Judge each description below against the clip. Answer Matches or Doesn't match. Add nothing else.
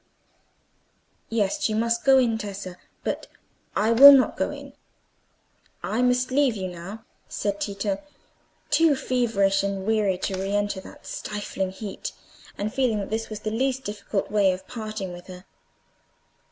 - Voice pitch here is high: Matches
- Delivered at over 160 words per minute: Doesn't match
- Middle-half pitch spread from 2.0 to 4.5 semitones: Matches